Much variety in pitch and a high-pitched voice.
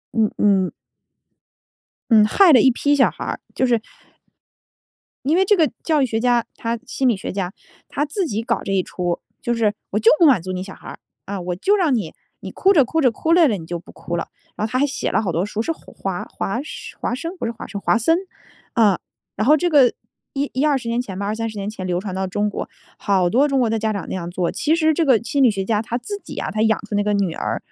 Yes: wide, 6.0 semitones; high, 225 Hz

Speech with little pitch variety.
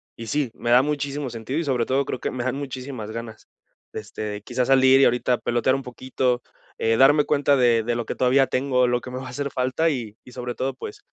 Yes: narrow, 2.1 semitones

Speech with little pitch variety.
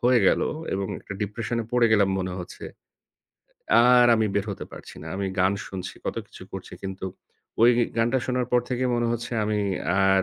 No: average, 3.8 semitones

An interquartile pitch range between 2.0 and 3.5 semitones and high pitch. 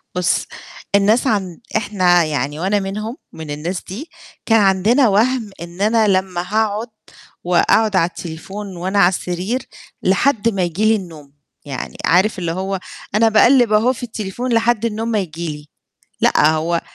No: average, 4.0 semitones; high, 195 Hz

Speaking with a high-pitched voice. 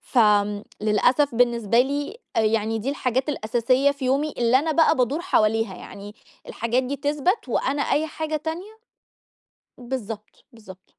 Yes: very high, 250 Hz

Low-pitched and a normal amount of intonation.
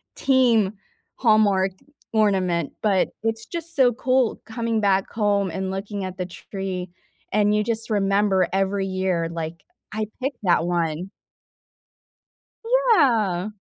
No: high, 200 Hz; average, 3.2 semitones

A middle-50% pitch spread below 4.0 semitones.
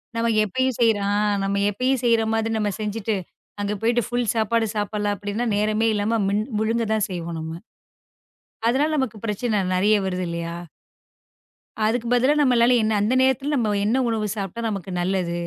Yes: narrow, 2.6 semitones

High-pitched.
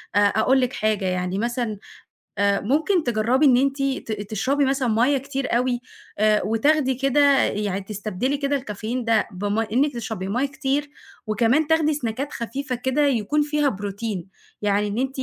Yes: high, 245 Hz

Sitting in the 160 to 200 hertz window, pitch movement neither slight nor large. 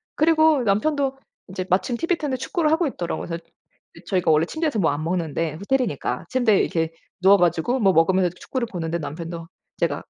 No: high, 190 Hz; wide, 8.0 semitones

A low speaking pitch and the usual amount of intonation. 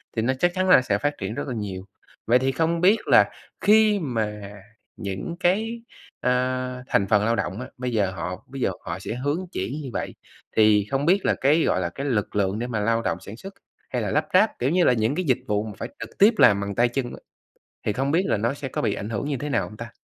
No: low, 120 Hz; wide, 5.9 semitones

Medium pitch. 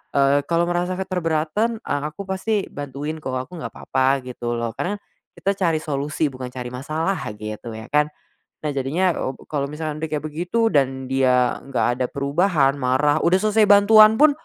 Yes: medium, 150 Hz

